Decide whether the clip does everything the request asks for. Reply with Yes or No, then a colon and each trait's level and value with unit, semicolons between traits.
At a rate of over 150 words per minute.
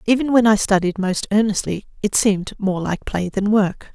Yes: average, 200 wpm